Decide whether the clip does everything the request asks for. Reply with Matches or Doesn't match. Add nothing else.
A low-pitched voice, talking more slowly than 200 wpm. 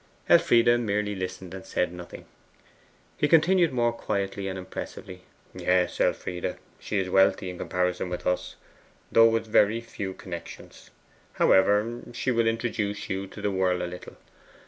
Matches